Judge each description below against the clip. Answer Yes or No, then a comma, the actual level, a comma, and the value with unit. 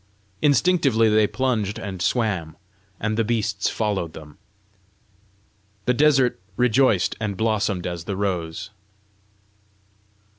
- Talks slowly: Yes, slow, 105 wpm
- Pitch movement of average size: Yes, average, 4.1 semitones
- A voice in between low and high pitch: No, low, 105 Hz